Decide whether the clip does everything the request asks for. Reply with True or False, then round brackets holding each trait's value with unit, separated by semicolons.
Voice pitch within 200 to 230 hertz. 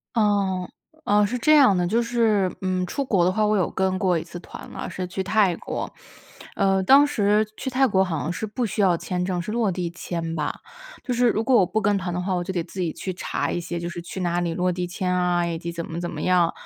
False (185 Hz)